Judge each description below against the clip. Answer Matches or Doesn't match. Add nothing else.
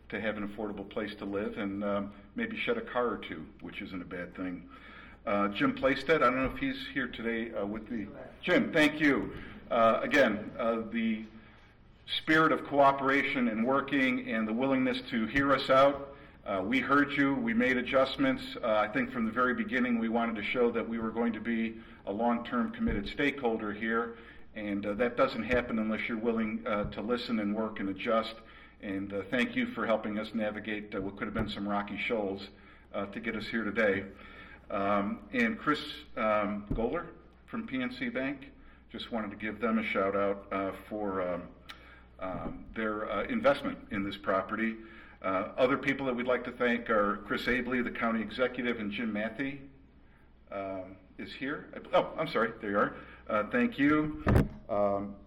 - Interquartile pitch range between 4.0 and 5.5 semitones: Matches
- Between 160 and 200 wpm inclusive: Matches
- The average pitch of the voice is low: Matches